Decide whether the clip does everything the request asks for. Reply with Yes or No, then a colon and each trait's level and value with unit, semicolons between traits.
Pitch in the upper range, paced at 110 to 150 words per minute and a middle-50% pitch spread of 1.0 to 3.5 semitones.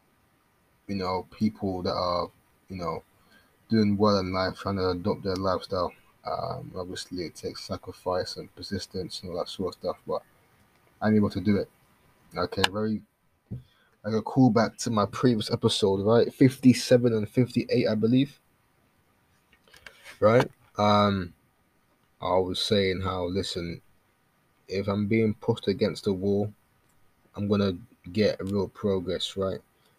No: low, 100 Hz; average, 140 wpm; average, 2.7 semitones